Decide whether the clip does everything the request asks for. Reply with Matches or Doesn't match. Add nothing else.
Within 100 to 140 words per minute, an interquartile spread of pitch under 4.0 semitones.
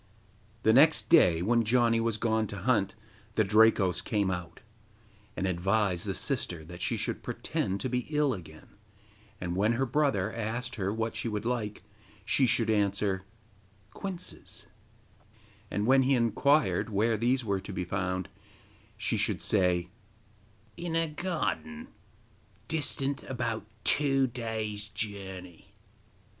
Doesn't match